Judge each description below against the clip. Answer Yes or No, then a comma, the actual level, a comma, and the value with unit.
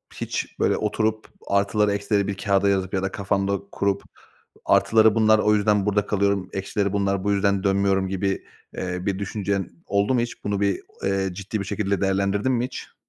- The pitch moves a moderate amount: No, narrow, 1.1 semitones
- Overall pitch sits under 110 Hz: Yes, low, 100 Hz